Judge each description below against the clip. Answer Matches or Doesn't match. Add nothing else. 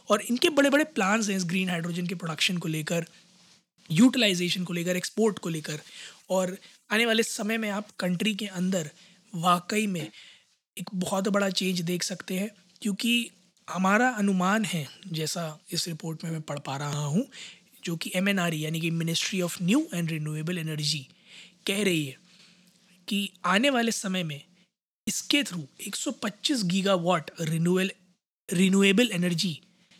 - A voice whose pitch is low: Doesn't match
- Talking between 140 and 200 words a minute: Matches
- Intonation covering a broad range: Doesn't match